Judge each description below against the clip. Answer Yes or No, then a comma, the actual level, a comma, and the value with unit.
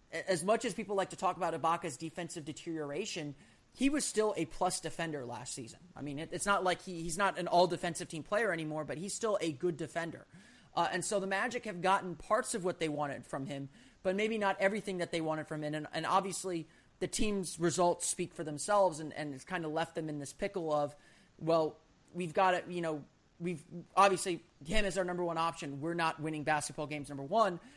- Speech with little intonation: No, average, 3.5 semitones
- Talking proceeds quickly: Yes, fast, 225 wpm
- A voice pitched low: No, medium, 170 Hz